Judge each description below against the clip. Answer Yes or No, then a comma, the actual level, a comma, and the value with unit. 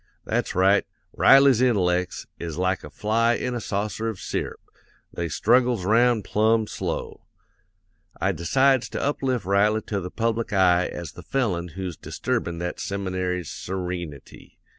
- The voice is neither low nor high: No, low, 100 Hz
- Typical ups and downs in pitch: Yes, average, 4.3 semitones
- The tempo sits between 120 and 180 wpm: Yes, average, 140 wpm